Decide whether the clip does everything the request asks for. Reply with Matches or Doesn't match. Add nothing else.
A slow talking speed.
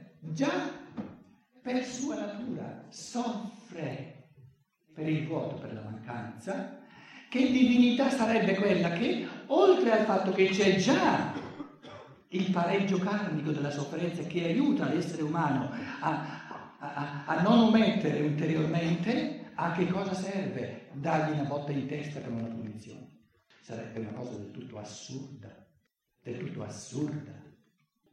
Doesn't match